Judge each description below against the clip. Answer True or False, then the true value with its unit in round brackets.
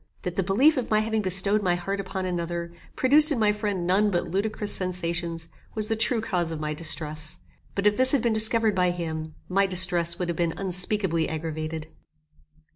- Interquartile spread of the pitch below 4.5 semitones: True (3.8 semitones)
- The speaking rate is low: False (195 wpm)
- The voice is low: False (185 Hz)